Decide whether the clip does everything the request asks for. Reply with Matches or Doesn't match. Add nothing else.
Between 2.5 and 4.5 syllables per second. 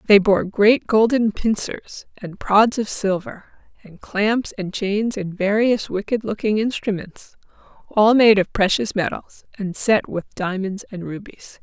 Matches